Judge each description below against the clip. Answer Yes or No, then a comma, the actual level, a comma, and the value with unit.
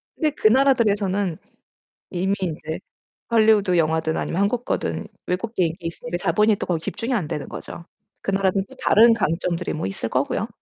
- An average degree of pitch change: Yes, average, 4.6 semitones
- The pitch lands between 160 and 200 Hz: Yes, high, 190 Hz